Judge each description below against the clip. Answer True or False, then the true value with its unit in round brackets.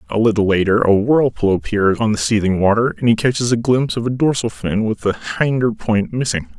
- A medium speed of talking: False (220 wpm)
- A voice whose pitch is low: True (110 Hz)